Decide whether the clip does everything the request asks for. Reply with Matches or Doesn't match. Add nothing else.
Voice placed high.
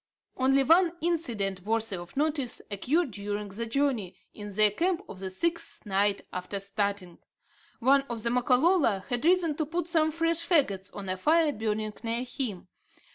Matches